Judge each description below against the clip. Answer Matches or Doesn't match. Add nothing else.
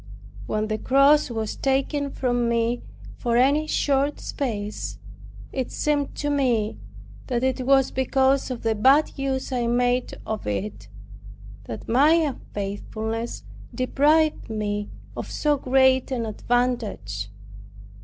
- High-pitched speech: Matches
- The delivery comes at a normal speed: Doesn't match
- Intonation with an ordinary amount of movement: Matches